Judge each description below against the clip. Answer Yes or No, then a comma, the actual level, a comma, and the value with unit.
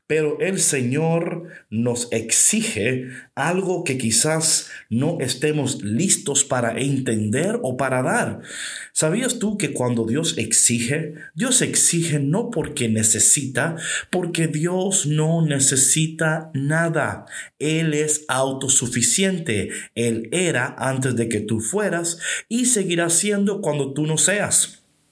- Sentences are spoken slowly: Yes, slow, 115 wpm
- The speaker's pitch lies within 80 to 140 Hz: No, medium, 150 Hz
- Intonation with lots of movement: No, average, 4.9 semitones